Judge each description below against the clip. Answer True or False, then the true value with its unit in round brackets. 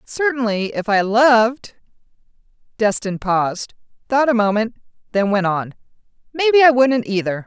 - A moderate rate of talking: False (130 wpm)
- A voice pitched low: False (225 Hz)